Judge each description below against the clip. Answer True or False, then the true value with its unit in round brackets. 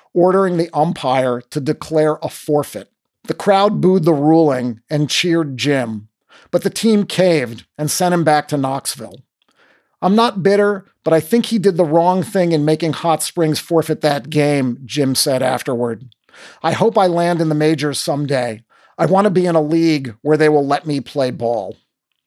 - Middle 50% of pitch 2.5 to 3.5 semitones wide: False (3.9 semitones)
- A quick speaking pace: False (185 wpm)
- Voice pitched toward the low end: False (155 Hz)